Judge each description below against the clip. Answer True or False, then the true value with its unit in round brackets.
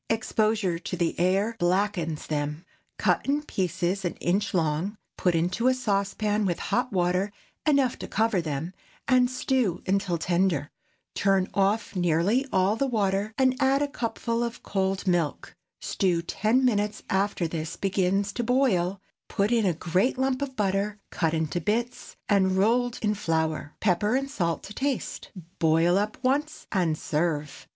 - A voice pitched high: True (195 Hz)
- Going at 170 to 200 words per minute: False (155 wpm)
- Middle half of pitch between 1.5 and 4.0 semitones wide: False (4.7 semitones)